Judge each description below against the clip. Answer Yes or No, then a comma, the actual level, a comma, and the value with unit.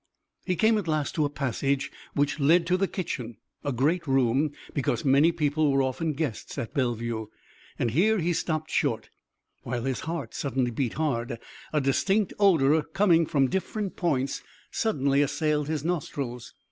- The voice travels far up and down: No, average, 4.0 semitones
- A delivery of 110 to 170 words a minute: Yes, average, 160 wpm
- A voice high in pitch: No, medium, 145 Hz